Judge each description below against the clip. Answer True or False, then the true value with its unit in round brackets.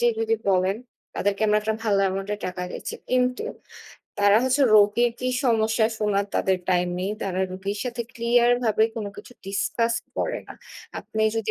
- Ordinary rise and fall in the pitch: True (3.1 semitones)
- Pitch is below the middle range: False (210 Hz)